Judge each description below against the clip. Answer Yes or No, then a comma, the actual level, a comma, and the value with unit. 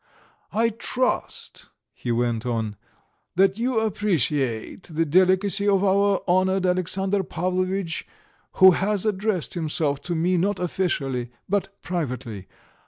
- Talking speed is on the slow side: Yes, slow, 115 wpm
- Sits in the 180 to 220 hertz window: Yes, medium, 185 Hz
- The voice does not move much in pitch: No, average, 4.7 semitones